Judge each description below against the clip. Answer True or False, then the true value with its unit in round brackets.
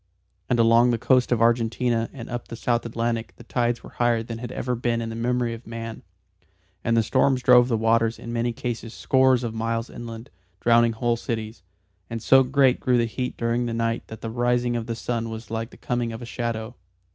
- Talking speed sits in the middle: False (215 wpm)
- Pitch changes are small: True (1.1 semitones)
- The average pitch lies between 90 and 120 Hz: True (115 Hz)